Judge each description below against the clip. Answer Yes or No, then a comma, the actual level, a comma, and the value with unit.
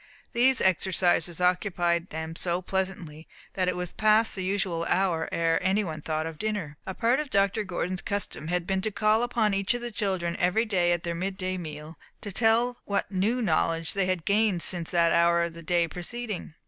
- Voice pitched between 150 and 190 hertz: Yes, medium, 185 Hz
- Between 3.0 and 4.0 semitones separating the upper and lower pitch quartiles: Yes, average, 3.4 semitones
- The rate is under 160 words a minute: No, average, 200 wpm